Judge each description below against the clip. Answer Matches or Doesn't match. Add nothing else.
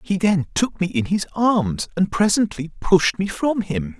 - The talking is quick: Doesn't match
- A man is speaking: Matches